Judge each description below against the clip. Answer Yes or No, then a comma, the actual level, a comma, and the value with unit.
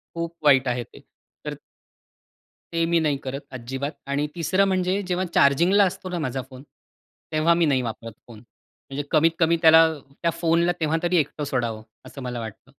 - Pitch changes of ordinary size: Yes, average, 4.2 semitones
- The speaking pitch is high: No, medium, 155 Hz